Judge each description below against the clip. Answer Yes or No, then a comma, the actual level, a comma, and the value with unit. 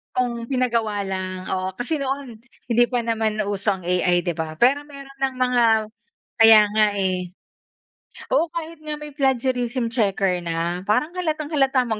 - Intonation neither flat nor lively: No, wide, 5.9 semitones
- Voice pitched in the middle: No, high, 235 Hz